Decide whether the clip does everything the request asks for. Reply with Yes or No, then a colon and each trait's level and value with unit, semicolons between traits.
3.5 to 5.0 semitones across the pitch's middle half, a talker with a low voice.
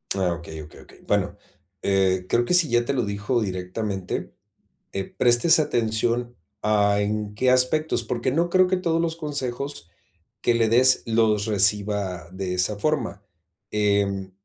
Yes: average, 4.3 semitones; low, 110 Hz